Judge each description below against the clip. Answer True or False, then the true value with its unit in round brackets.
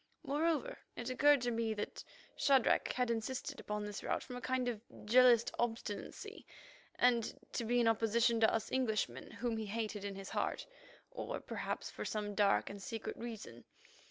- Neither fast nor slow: True (170 wpm)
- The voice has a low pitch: False (230 Hz)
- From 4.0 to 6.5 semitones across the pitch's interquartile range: False (2.8 semitones)